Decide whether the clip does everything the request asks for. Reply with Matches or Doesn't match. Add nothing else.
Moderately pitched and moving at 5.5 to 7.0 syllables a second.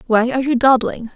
Doesn't match